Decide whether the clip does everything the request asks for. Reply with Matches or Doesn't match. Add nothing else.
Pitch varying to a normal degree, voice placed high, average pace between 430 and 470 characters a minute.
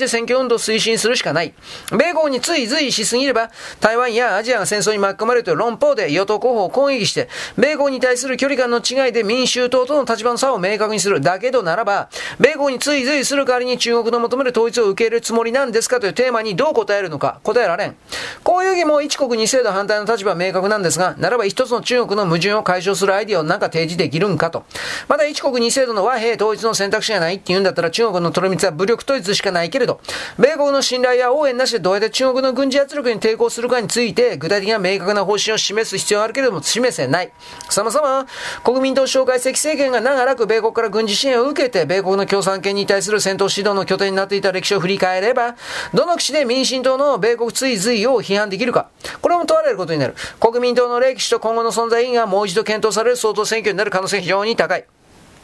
Matches